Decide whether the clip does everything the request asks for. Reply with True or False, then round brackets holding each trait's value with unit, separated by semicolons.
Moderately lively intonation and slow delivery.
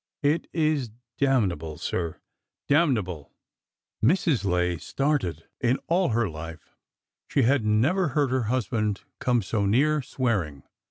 False (7.5 semitones; 125 wpm)